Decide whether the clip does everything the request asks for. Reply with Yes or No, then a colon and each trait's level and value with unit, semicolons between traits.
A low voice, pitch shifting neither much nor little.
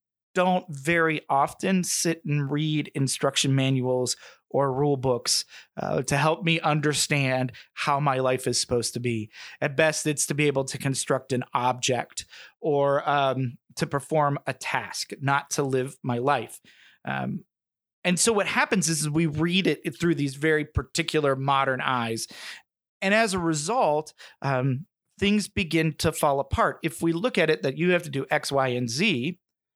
No: medium, 145 Hz; average, 3.6 semitones